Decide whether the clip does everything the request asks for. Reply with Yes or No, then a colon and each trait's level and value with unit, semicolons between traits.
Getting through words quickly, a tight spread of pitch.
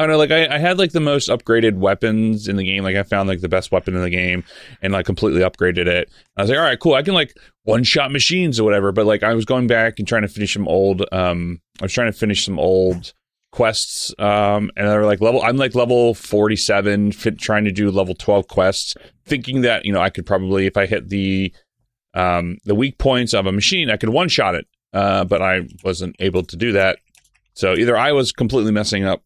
No: fast, 245 wpm; average, 3.2 semitones